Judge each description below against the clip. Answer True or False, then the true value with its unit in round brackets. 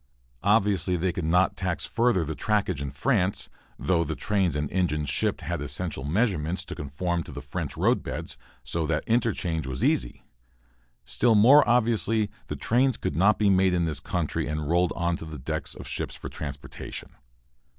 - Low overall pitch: True (90 Hz)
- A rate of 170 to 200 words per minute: True (175 wpm)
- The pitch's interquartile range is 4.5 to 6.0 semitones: True (5.1 semitones)